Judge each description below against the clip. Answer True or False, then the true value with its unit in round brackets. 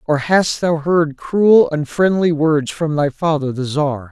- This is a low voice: False (155 Hz)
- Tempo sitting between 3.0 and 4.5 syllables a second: True (3.8 syllables/s)